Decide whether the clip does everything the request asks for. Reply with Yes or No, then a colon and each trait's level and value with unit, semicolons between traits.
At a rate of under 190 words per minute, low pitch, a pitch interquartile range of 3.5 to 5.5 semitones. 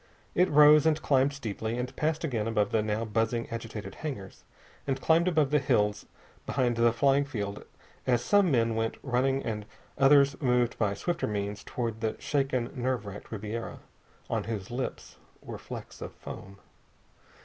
Yes: average, 160 wpm; low, 120 Hz; average, 4.0 semitones